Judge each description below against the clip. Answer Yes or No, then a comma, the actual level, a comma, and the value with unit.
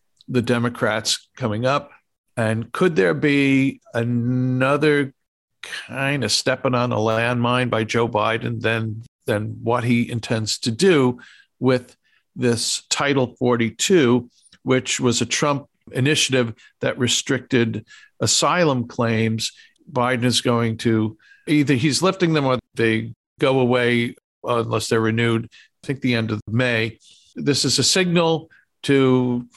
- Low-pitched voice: Yes, low, 120 Hz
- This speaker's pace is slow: Yes, slow, 130 wpm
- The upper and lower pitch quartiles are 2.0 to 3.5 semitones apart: Yes, average, 2.8 semitones